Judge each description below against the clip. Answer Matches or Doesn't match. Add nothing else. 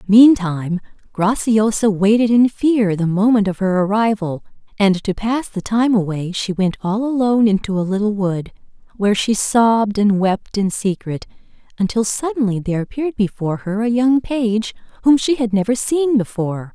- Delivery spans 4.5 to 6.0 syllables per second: Matches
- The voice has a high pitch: Matches